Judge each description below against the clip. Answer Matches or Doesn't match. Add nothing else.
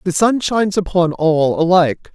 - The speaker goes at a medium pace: Matches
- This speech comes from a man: Matches